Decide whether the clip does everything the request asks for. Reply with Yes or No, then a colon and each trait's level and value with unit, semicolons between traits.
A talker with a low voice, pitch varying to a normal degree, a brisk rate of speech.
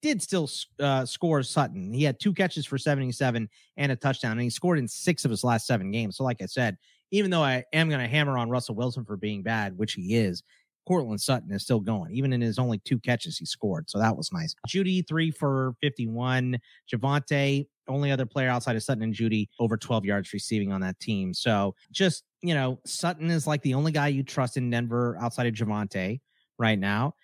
Yes: low, 125 Hz; average, 4.4 semitones; fast, 220 wpm